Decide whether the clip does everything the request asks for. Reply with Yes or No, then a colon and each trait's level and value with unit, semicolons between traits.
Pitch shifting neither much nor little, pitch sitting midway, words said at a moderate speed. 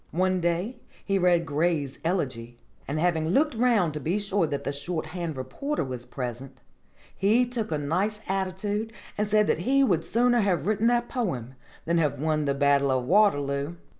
No: wide, 6.7 semitones; medium, 175 Hz; average, 175 wpm